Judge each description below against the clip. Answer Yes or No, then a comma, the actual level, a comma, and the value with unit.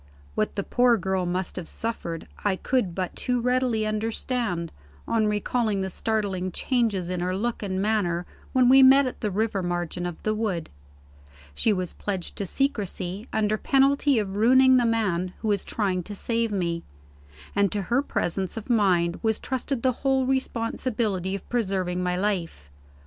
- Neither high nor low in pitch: No, high, 210 Hz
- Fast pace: No, average, 170 wpm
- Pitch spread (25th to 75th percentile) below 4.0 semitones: No, average, 4.3 semitones